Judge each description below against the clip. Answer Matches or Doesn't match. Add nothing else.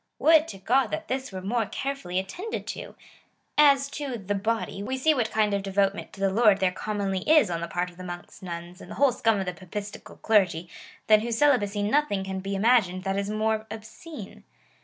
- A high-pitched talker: Matches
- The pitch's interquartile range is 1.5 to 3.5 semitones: Doesn't match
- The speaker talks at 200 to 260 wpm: Matches